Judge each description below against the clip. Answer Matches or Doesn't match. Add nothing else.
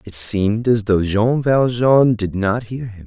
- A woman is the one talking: Doesn't match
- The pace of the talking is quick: Doesn't match